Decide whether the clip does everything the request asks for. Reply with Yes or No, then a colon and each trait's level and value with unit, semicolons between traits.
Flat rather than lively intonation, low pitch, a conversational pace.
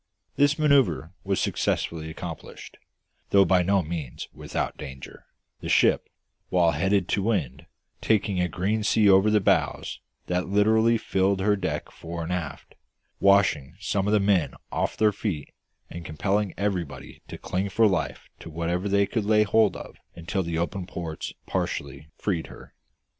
No: average, 3.5 semitones; very low, 95 Hz; average, 160 wpm